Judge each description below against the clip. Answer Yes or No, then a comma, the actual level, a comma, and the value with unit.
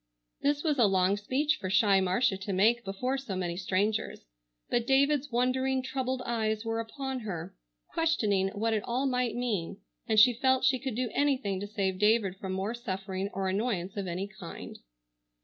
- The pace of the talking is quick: No, average, 180 wpm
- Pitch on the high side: Yes, high, 220 Hz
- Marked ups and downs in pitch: No, average, 4.8 semitones